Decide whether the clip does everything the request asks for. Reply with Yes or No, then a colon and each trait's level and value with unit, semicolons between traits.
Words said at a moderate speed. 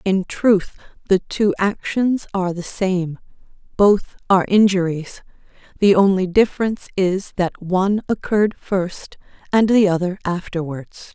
No: slow, 125 wpm